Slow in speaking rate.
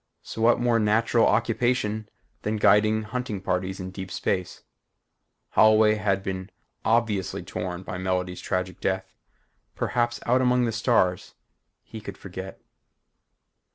Yes: slow, 125 wpm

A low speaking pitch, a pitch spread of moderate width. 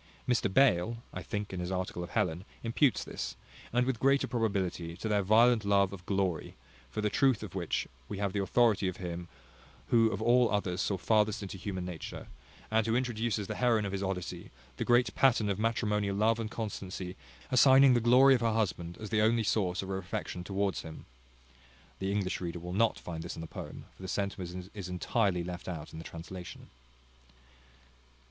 Yes: low, 100 Hz; average, 3.8 semitones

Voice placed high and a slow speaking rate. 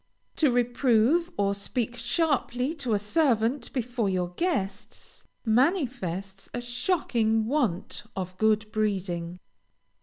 Yes: high, 230 Hz; slow, 110 wpm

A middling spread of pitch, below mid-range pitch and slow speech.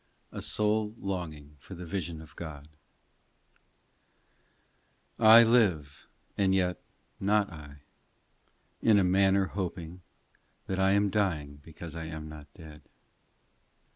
Yes: average, 4.3 semitones; very low, 90 Hz; slow, 115 wpm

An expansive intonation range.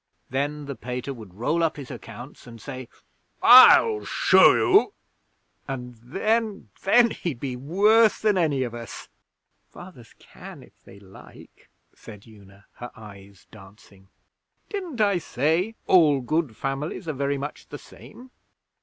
Yes: wide, 7.9 semitones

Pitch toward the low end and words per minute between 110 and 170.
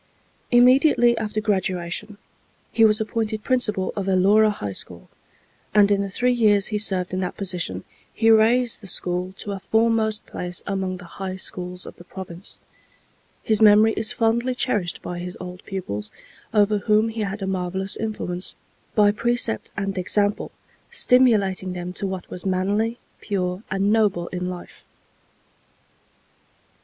No: high, 200 Hz; average, 150 wpm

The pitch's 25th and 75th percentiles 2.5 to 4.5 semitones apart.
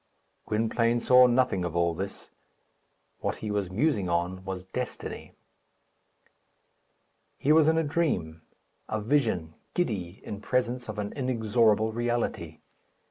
No: average, 5.3 semitones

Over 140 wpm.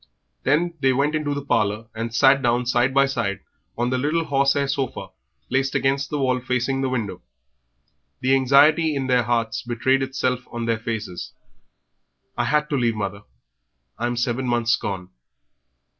Yes: average, 160 wpm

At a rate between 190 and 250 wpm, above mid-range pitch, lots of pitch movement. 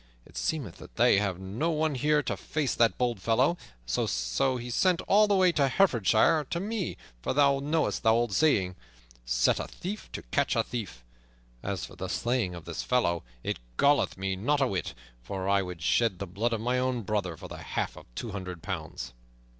No: fast, 205 wpm; low, 115 Hz; wide, 7.4 semitones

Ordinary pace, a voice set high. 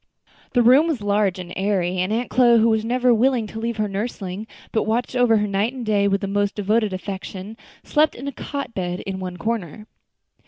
No: fast, 210 wpm; high, 215 Hz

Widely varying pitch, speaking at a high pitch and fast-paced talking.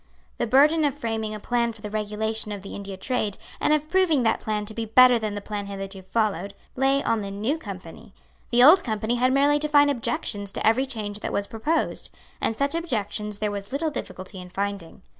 No: average, 4.8 semitones; high, 220 Hz; fast, 215 wpm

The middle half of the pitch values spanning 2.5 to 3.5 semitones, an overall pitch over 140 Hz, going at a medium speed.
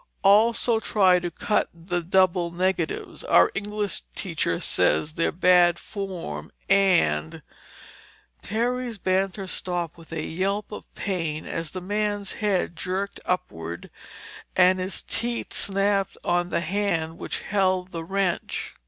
No: average, 2.8 semitones; medium, 185 Hz; slow, 125 wpm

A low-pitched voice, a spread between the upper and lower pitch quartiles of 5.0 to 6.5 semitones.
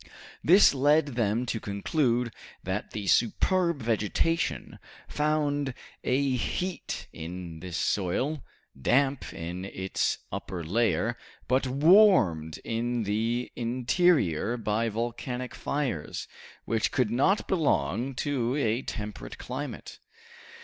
Yes: low, 120 Hz; wide, 5.5 semitones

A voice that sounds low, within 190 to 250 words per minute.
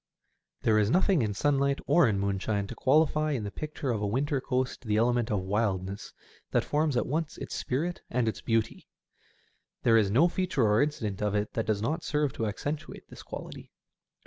Yes: low, 120 Hz; average, 195 wpm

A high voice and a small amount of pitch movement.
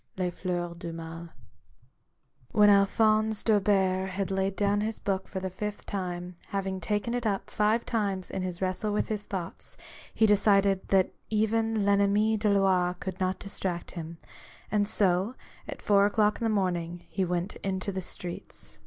Yes: high, 195 Hz; narrow, 2.3 semitones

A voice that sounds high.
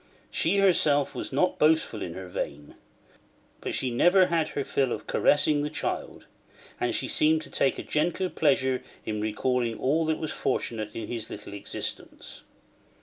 No: medium, 140 Hz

